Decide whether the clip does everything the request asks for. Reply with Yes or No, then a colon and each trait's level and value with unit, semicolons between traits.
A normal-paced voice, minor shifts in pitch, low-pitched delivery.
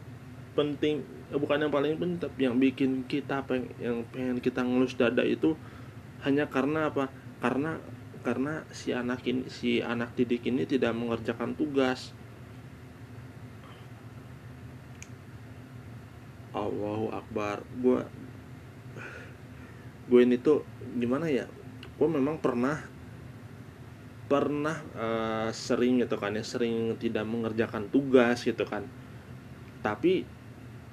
Yes: average, 105 wpm; narrow, 1.3 semitones; low, 125 Hz